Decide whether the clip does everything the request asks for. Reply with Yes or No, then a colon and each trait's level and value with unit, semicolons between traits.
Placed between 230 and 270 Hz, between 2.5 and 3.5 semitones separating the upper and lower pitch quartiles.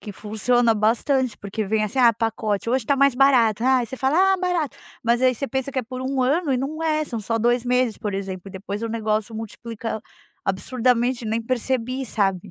Yes: high, 235 Hz; average, 3.2 semitones